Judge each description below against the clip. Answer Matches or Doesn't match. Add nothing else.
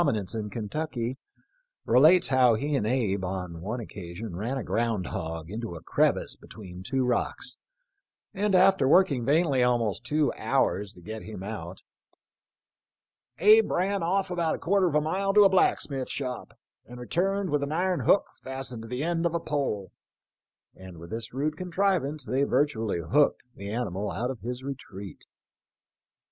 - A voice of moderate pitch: Doesn't match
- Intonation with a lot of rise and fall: Matches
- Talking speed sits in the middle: Matches